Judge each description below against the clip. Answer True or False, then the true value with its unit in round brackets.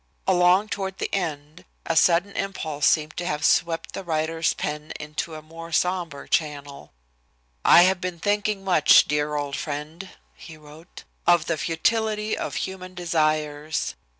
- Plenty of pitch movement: False (3.4 semitones)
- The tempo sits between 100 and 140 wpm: False (150 wpm)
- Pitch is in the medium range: True (165 Hz)